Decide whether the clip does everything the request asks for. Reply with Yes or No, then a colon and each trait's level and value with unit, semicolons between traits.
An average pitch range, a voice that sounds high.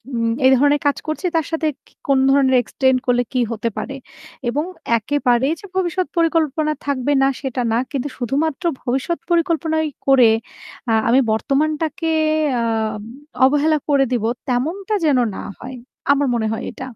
Yes: average, 4.0 semitones; very high, 275 Hz